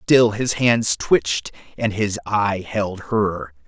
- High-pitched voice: No, low, 105 Hz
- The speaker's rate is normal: Yes, average, 145 wpm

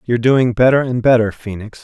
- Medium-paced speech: Yes, average, 195 wpm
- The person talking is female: No, male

